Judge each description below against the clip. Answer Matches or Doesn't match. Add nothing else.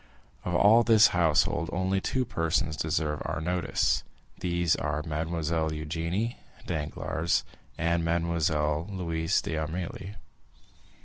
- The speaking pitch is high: Doesn't match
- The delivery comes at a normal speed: Doesn't match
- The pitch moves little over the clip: Matches